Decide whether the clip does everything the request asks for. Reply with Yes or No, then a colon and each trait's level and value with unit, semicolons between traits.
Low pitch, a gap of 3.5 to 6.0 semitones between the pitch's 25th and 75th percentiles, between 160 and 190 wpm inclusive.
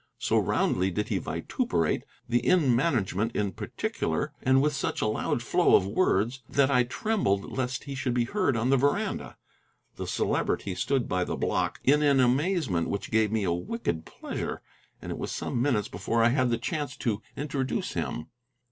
Yes: low, 125 Hz; average, 5.0 semitones; average, 185 wpm